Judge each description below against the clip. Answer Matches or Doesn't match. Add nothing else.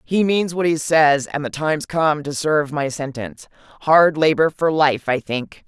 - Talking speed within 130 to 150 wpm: Doesn't match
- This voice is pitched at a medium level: Matches